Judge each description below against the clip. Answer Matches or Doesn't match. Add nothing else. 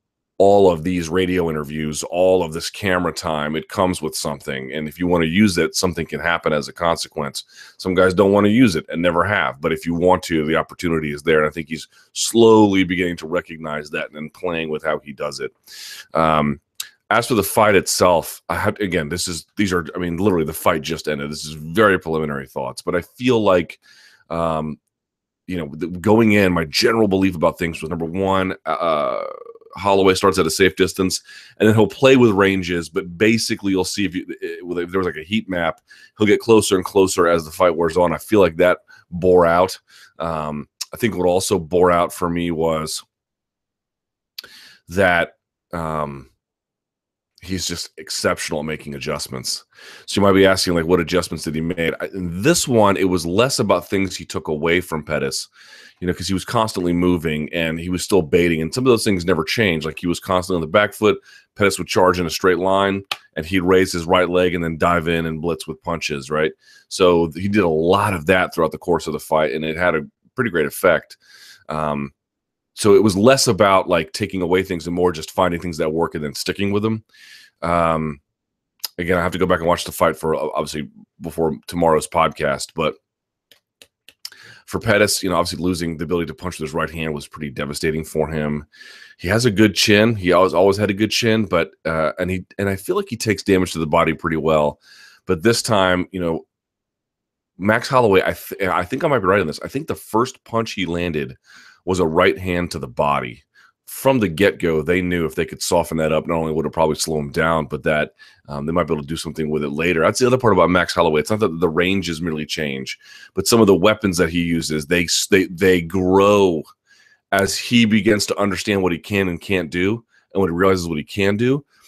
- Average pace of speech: Doesn't match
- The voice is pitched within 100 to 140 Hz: Doesn't match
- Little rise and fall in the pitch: Doesn't match